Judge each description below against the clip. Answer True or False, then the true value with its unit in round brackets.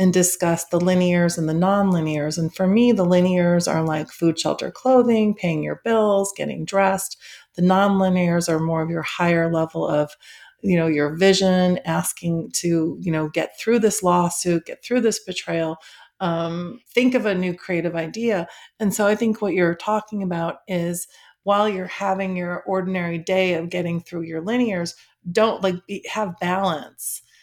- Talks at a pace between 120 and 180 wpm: True (175 wpm)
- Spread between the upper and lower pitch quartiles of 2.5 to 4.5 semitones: True (2.8 semitones)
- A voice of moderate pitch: True (180 Hz)